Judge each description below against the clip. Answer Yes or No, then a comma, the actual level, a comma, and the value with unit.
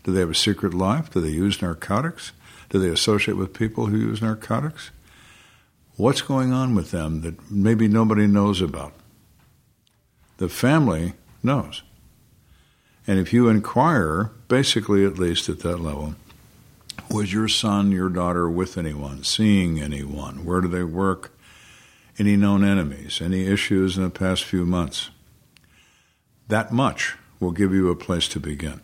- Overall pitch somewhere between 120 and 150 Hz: No, very low, 95 Hz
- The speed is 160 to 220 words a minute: No, average, 150 wpm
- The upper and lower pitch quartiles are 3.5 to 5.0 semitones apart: Yes, average, 3.9 semitones